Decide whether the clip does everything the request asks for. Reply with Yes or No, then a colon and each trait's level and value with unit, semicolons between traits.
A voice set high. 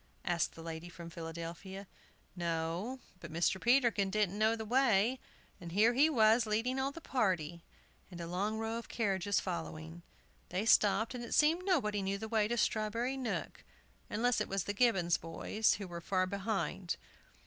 Yes: high, 205 Hz